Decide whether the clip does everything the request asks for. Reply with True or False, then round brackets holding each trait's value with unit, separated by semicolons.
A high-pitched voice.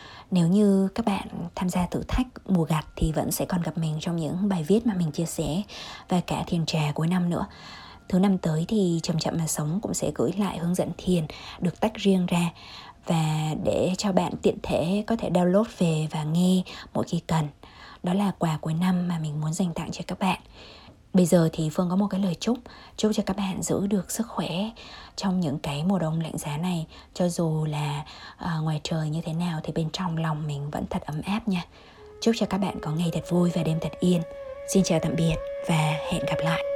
False (175 Hz)